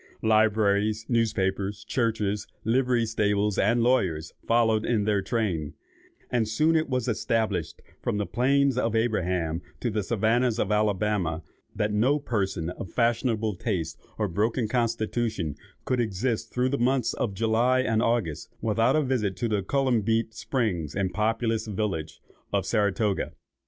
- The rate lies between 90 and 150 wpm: Yes, average, 140 wpm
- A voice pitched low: Yes, low, 110 Hz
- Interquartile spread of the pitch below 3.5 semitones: Yes, average, 2.9 semitones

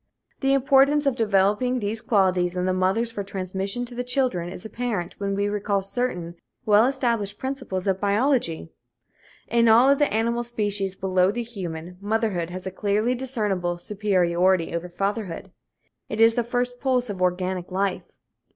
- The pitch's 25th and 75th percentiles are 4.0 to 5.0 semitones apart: Yes, average, 4.5 semitones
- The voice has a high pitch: Yes, high, 205 Hz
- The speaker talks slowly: No, average, 160 wpm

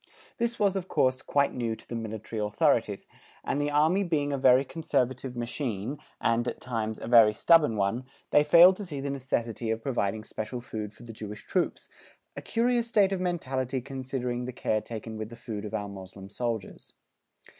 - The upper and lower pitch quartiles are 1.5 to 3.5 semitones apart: No, average, 4.9 semitones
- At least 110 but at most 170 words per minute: No, average, 190 wpm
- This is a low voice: Yes, low, 125 Hz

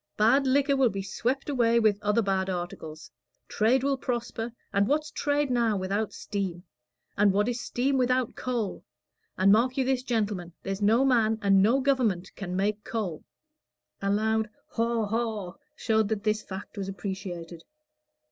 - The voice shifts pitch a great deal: No, average, 4.0 semitones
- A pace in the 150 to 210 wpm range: Yes, average, 160 wpm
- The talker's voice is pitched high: Yes, high, 220 Hz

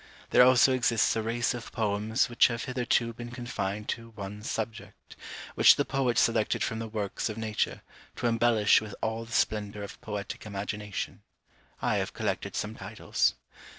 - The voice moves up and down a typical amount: No, narrow, 2.1 semitones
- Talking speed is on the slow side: No, average, 165 wpm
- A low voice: Yes, low, 110 Hz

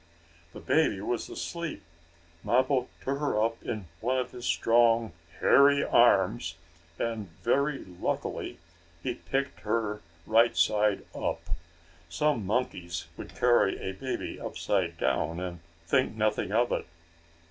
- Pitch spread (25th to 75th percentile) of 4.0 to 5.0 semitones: Yes, average, 4.3 semitones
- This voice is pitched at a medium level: No, low, 115 Hz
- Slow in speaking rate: Yes, slow, 125 wpm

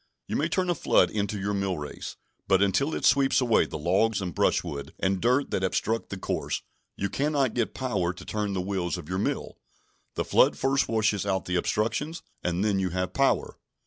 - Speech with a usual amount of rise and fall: Yes, average, 4.6 semitones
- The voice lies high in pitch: No, low, 100 Hz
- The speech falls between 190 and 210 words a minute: Yes, average, 200 wpm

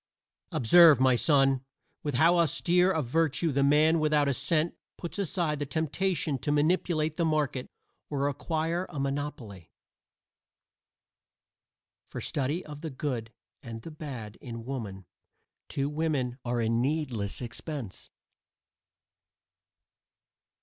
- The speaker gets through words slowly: Yes, slow, 120 wpm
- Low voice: No, medium, 145 Hz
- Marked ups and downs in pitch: No, average, 3.8 semitones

